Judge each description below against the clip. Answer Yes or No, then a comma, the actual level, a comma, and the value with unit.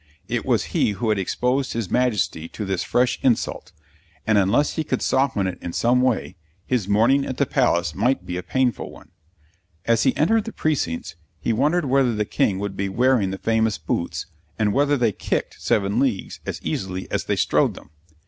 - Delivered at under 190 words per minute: No, average, 195 wpm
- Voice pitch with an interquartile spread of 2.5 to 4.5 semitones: No, average, 5.1 semitones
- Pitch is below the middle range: Yes, low, 115 Hz